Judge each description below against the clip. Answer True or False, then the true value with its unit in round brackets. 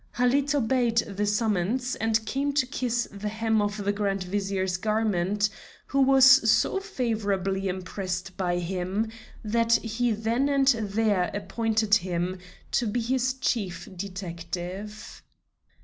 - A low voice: False (215 Hz)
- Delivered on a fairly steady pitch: False (3.7 semitones)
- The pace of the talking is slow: True (130 wpm)